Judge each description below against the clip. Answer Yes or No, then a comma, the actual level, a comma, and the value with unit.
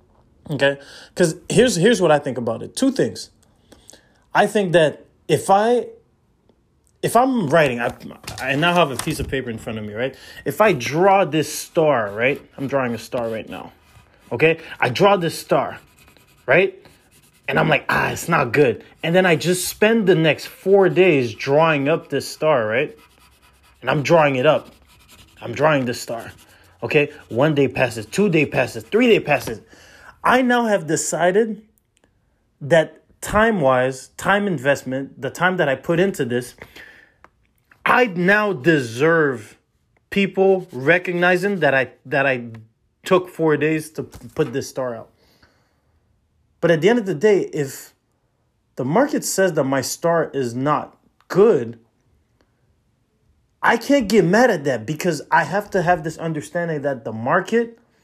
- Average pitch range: No, wide, 6.8 semitones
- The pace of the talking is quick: No, average, 160 wpm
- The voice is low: No, medium, 155 Hz